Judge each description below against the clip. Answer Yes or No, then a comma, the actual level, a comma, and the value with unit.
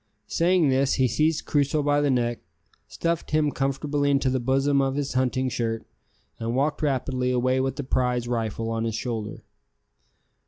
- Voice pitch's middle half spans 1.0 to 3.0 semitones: Yes, average, 2.7 semitones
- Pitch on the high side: No, low, 130 Hz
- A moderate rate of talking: Yes, average, 165 wpm